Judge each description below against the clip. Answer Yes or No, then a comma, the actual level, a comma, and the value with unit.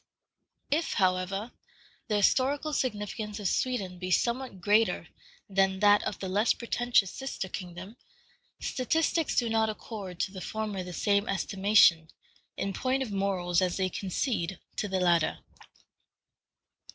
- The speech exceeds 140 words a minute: No, slow, 135 wpm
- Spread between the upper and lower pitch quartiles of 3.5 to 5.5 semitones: Yes, average, 3.9 semitones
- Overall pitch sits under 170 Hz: No, high, 205 Hz